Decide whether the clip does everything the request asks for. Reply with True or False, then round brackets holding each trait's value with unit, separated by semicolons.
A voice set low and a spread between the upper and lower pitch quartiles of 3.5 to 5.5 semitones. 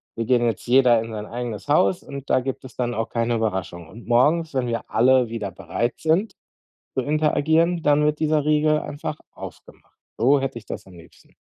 True (130 Hz; 4.5 semitones)